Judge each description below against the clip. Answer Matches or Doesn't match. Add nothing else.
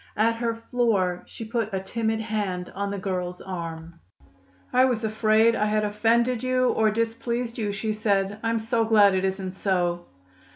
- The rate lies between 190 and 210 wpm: Doesn't match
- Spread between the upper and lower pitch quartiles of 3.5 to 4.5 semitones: Doesn't match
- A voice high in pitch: Matches